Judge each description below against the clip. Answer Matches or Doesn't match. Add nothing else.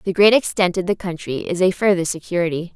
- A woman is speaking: Matches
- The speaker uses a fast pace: Matches